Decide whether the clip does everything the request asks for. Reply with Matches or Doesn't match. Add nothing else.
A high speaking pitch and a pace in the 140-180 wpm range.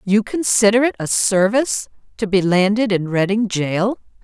Matches